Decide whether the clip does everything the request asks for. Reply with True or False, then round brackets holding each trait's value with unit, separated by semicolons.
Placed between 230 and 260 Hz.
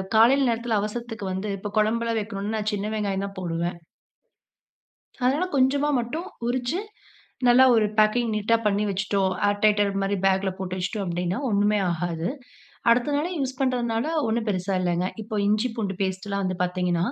False (210 Hz)